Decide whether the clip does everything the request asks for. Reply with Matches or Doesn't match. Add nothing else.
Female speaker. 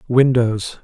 Doesn't match